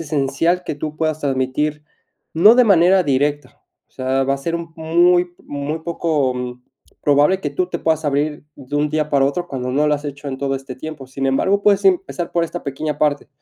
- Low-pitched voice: No, medium, 150 Hz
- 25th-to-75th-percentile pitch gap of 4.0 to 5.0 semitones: No, average, 3.5 semitones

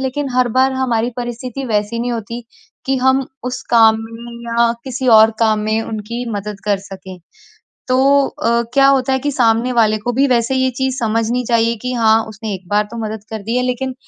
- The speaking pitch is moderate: No, high, 235 Hz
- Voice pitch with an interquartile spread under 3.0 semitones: Yes, narrow, 2.5 semitones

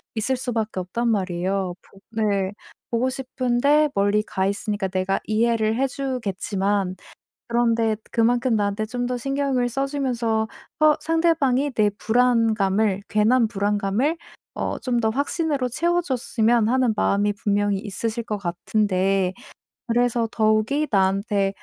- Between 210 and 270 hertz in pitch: Yes, high, 225 Hz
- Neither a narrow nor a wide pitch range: Yes, average, 3.8 semitones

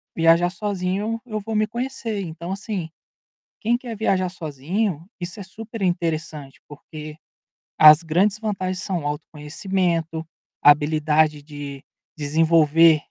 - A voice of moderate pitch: Yes, medium, 170 Hz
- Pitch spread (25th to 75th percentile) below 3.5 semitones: No, average, 4.6 semitones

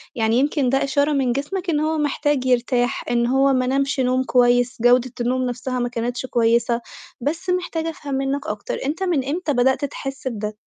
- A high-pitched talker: Yes, very high, 260 Hz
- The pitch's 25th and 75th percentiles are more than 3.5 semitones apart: No, average, 2.8 semitones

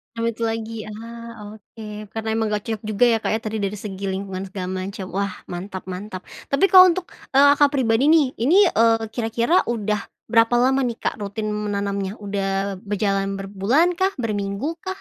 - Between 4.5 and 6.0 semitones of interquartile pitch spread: No, average, 2.9 semitones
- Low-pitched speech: No, high, 215 Hz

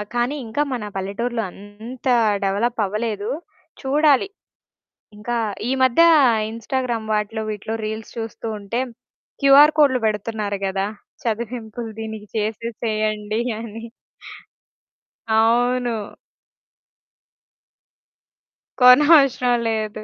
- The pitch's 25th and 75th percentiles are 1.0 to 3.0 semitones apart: Yes, narrow, 2.5 semitones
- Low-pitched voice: No, high, 225 Hz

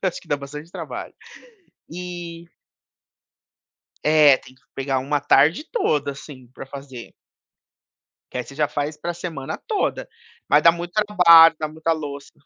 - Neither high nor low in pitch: Yes, medium, 150 Hz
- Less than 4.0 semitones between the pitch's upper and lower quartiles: Yes, average, 3.3 semitones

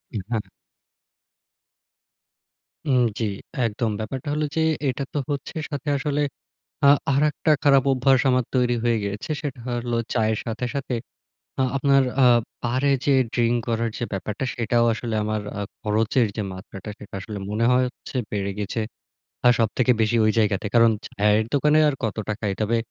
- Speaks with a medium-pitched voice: No, low, 120 Hz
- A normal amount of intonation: Yes, average, 3.6 semitones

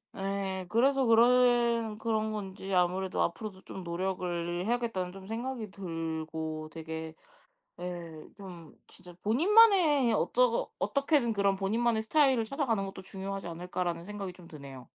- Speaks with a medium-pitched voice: No, high, 195 Hz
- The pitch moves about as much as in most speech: Yes, average, 4.9 semitones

